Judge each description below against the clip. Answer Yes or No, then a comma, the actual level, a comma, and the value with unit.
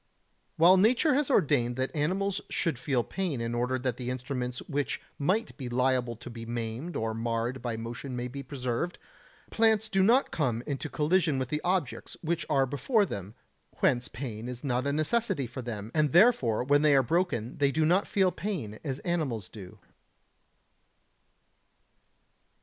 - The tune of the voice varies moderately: No, wide, 6.2 semitones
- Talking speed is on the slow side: No, average, 165 wpm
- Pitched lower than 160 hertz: Yes, low, 135 Hz